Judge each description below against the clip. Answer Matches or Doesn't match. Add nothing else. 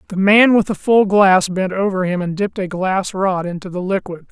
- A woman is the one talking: Doesn't match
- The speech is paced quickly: Matches